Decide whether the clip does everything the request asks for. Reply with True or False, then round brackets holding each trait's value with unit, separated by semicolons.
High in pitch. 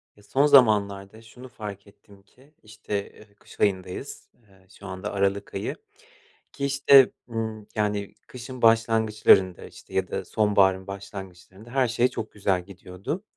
False (105 Hz)